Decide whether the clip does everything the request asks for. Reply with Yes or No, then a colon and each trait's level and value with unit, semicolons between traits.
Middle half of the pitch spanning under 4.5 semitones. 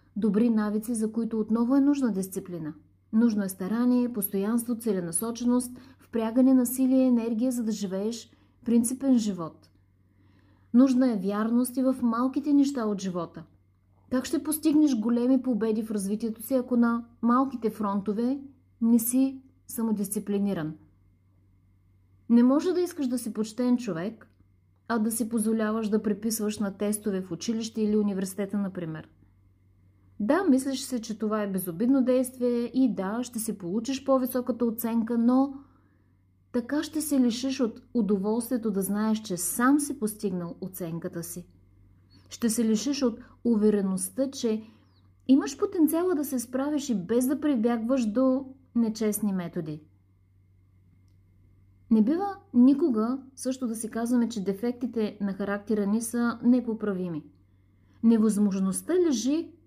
No: average, 4.8 semitones